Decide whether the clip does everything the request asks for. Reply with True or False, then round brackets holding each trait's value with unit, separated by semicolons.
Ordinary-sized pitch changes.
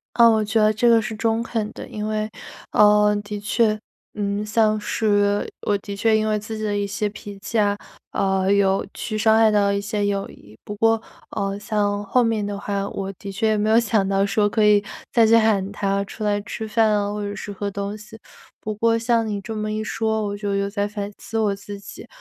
False (1.4 semitones)